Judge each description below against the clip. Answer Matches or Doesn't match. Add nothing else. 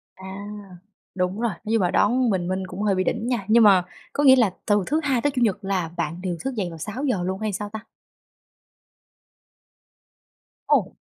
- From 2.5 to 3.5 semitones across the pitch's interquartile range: Doesn't match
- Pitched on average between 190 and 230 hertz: Matches